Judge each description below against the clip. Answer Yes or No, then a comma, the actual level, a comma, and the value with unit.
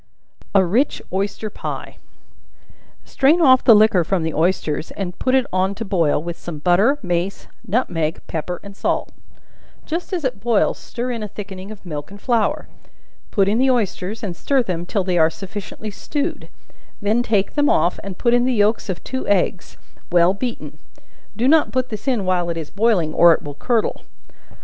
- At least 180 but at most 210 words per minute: Yes, average, 185 wpm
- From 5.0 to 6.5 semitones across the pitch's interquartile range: Yes, average, 5.3 semitones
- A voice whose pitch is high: Yes, high, 200 Hz